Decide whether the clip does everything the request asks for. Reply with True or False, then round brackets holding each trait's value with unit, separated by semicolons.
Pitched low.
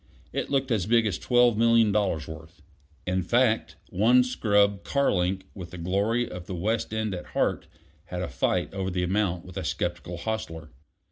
True (100 Hz)